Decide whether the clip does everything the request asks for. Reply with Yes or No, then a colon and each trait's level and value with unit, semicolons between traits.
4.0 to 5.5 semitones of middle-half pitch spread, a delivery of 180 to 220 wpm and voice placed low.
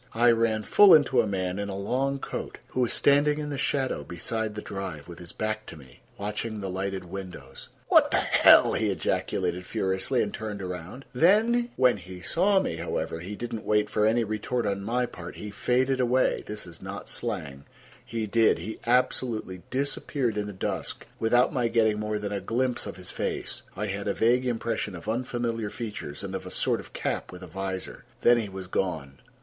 Yes: average, 4.3 semitones; average, 195 wpm; low, 105 Hz